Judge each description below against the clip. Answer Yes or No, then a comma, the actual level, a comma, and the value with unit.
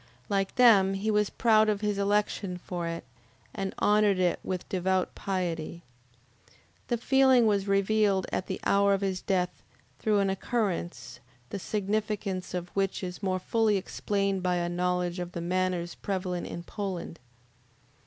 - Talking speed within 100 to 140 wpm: No, average, 155 wpm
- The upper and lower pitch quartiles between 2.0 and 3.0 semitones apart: Yes, narrow, 2.4 semitones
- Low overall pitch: No, high, 195 Hz